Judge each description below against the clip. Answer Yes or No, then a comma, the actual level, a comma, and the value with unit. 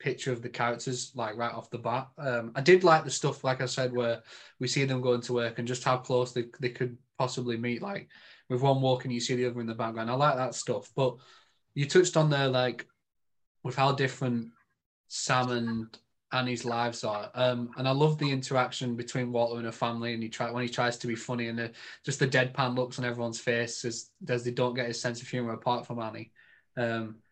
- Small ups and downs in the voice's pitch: Yes, narrow, 1.6 semitones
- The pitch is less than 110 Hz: No, low, 125 Hz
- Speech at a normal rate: No, fast, 230 wpm